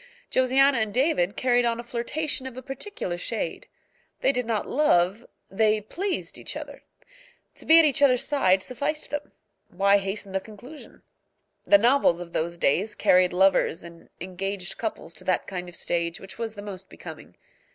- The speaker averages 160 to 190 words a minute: Yes, average, 170 wpm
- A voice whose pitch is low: No, high, 215 Hz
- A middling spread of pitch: No, wide, 5.9 semitones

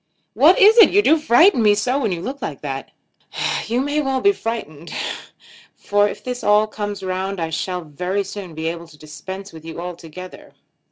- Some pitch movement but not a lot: No, wide, 6.4 semitones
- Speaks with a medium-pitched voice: No, high, 200 Hz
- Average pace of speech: Yes, average, 190 wpm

